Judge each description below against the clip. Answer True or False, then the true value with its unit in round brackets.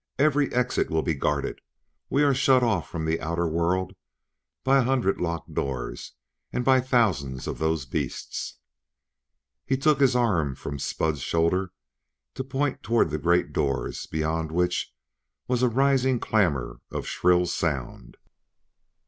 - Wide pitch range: True (8.1 semitones)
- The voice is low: True (90 Hz)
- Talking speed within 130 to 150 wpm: True (145 wpm)